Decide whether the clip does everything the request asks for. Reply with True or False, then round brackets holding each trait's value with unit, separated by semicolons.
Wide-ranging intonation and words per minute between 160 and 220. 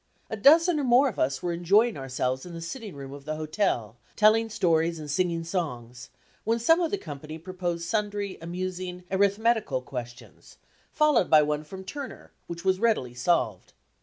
True (6.2 semitones; 170 wpm)